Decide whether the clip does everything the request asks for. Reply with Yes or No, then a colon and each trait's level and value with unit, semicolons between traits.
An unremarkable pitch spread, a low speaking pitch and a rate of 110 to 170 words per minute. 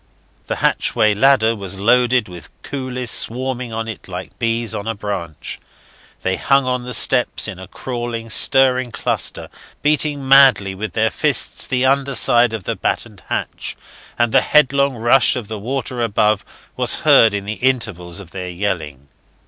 Yes: average, 4.2 semitones; low, 115 Hz; average, 160 wpm